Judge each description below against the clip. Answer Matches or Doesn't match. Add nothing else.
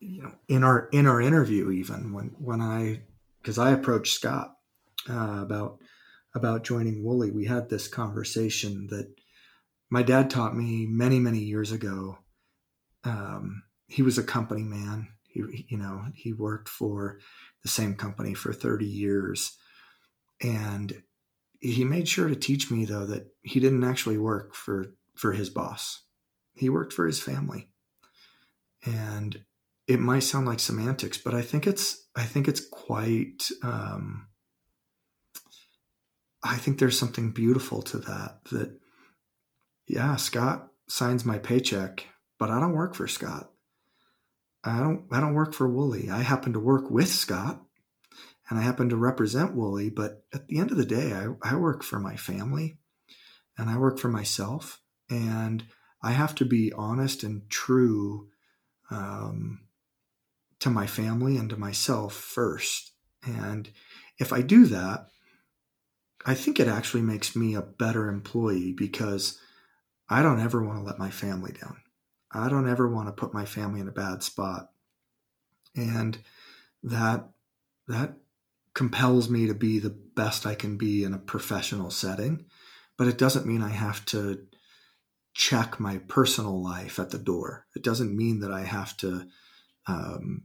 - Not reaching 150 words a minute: Doesn't match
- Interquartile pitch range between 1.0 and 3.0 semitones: Doesn't match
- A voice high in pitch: Doesn't match